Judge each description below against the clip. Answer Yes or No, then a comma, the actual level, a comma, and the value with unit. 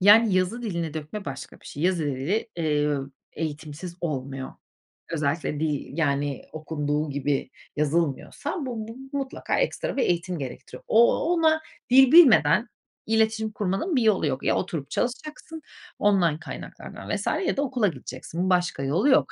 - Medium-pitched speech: Yes, medium, 170 Hz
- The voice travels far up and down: Yes, wide, 7.4 semitones